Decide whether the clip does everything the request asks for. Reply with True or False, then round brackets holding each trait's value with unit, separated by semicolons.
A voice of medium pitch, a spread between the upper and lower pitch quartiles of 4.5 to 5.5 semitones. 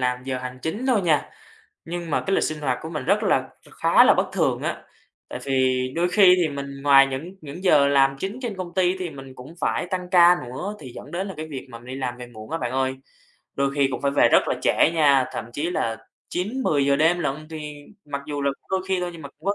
True (150 Hz; 4.8 semitones)